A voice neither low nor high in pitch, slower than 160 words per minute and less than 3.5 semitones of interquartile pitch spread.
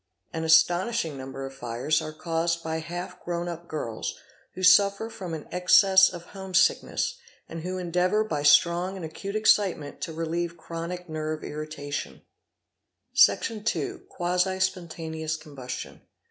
Yes: medium, 170 Hz; average, 140 wpm; average, 2.9 semitones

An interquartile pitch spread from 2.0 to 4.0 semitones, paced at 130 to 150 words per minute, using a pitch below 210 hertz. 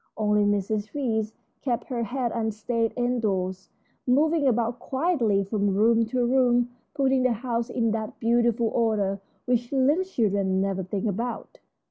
No: average, 3.0 semitones; average, 145 wpm; high, 230 Hz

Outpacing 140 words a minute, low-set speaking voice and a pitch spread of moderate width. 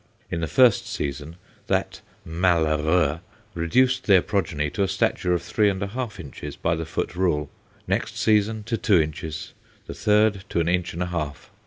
Yes: average, 180 wpm; very low, 90 Hz; average, 4.2 semitones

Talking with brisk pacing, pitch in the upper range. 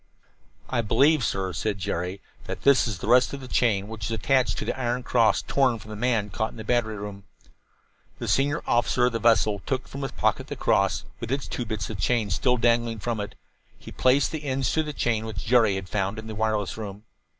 No: fast, 230 wpm; low, 115 Hz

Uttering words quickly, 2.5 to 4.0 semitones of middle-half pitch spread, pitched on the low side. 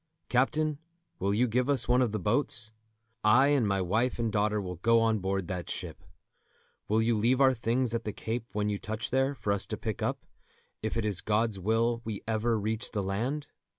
Yes: fast, 210 wpm; average, 2.8 semitones; low, 110 Hz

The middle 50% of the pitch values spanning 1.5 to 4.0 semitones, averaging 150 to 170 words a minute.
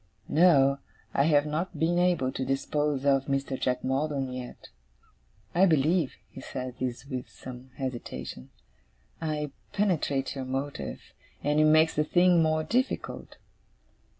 No: average, 3.1 semitones; slow, 135 wpm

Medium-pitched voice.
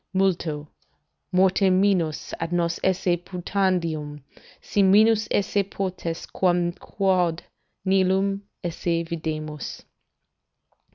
Yes: medium, 180 Hz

